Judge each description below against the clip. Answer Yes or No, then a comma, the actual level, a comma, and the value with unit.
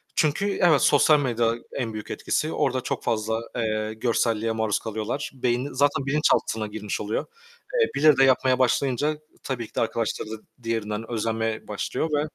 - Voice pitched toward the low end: Yes, low, 120 Hz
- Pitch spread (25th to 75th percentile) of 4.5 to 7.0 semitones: No, average, 3.9 semitones